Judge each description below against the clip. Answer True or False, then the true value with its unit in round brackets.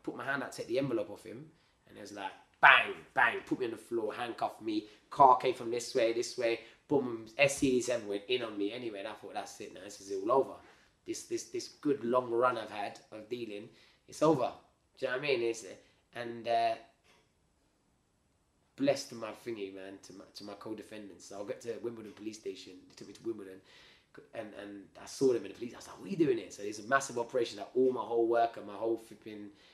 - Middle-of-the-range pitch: False (115 Hz)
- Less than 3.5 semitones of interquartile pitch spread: False (5.3 semitones)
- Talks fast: True (235 wpm)